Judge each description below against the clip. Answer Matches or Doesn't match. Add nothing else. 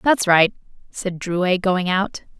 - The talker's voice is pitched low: Doesn't match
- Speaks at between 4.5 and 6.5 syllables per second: Doesn't match